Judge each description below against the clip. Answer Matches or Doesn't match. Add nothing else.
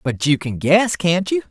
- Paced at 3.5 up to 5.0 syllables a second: Matches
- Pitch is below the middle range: Doesn't match